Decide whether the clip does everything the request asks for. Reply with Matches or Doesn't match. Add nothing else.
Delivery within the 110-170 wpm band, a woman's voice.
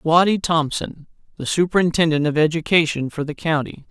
Doesn't match